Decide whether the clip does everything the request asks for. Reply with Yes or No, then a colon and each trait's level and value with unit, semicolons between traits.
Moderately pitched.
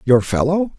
Yes: medium, 145 Hz